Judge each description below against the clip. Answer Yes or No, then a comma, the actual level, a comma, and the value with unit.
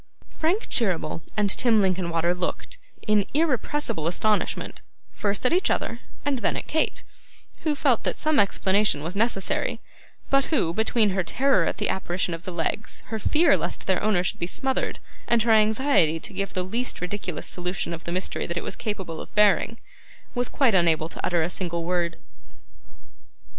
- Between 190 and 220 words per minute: No, average, 175 wpm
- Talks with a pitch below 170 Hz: No, high, 200 Hz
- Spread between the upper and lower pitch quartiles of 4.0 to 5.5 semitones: Yes, average, 5.2 semitones